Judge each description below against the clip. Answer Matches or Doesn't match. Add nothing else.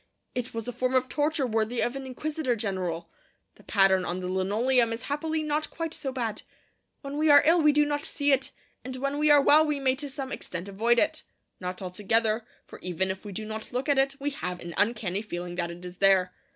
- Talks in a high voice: Matches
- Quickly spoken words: Matches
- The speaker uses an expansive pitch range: Matches